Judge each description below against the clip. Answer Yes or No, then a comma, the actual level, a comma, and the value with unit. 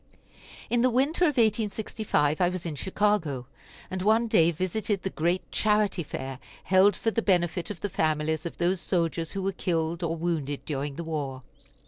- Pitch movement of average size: Yes, average, 4.6 semitones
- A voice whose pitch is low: No, medium, 180 Hz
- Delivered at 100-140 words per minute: No, average, 175 wpm